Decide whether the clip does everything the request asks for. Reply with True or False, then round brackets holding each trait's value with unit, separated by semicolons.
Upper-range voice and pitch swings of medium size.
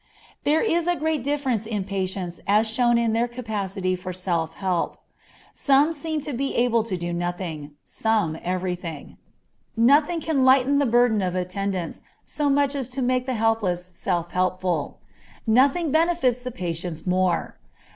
False (220 Hz; 6.7 semitones)